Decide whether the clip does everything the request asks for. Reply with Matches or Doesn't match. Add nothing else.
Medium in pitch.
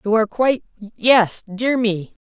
Doesn't match